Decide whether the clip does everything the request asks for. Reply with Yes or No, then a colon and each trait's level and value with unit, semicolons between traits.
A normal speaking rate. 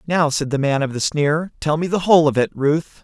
No: fast, 275 wpm